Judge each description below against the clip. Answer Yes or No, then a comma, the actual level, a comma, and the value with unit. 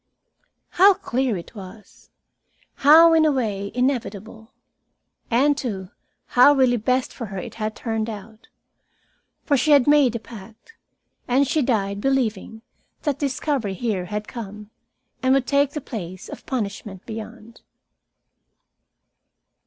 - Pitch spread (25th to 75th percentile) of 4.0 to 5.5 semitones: Yes, average, 4.5 semitones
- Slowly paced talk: Yes, slow, 130 wpm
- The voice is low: No, high, 235 Hz